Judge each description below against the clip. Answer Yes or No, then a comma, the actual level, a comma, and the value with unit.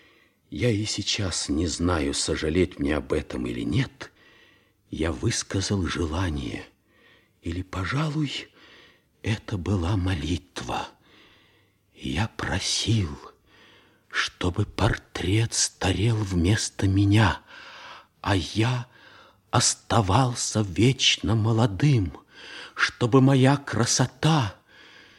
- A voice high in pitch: No, low, 105 Hz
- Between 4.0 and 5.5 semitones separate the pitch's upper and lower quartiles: Yes, average, 4.5 semitones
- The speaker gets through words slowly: Yes, slow, 80 wpm